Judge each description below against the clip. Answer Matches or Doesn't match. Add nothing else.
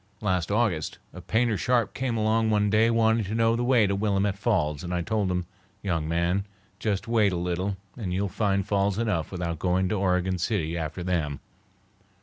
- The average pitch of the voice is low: Matches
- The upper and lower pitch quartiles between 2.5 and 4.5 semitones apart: Matches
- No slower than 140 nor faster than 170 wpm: Doesn't match